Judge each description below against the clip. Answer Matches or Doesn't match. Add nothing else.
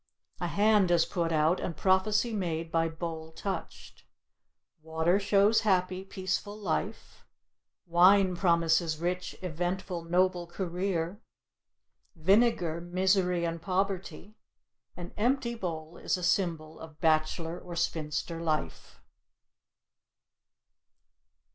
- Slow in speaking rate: Matches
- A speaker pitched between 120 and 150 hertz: Doesn't match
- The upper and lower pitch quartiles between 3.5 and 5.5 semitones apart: Doesn't match